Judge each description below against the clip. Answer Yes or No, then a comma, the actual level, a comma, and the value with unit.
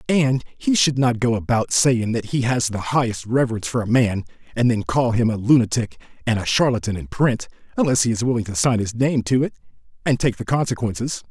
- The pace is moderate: No, fast, 220 wpm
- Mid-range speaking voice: No, low, 120 Hz